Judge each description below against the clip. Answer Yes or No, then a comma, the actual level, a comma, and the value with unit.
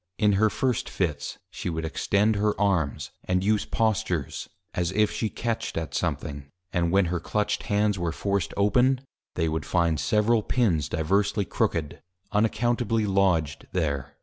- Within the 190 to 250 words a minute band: No, average, 150 wpm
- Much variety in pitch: No, average, 4.6 semitones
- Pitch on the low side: Yes, low, 100 Hz